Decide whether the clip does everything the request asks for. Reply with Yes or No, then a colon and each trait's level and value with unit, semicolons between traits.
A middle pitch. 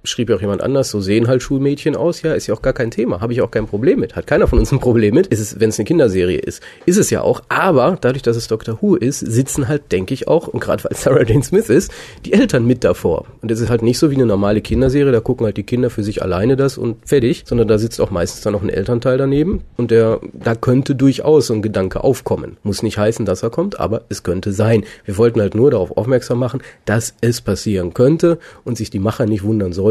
No: low, 115 Hz